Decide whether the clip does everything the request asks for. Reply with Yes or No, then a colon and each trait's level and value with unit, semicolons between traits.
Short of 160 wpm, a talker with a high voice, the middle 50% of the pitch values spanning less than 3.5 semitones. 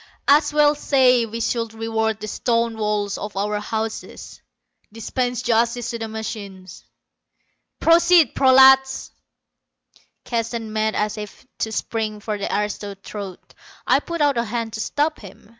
Yes: average, 140 wpm; high, 225 Hz; average, 2.9 semitones